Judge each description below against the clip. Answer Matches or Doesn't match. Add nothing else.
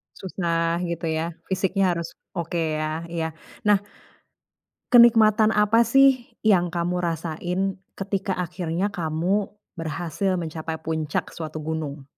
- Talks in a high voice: Doesn't match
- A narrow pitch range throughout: Doesn't match